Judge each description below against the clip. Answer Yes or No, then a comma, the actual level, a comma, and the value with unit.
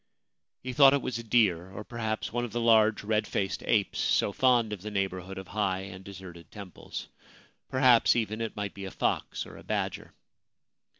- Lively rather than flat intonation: No, average, 3.3 semitones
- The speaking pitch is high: No, low, 105 Hz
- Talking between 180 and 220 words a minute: Yes, average, 190 wpm